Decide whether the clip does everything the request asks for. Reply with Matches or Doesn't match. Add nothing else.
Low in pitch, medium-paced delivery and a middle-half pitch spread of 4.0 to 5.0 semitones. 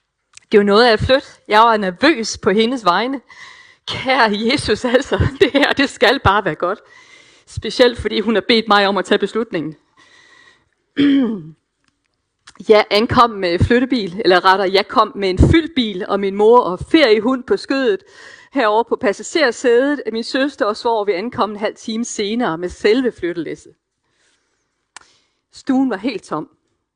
Doesn't match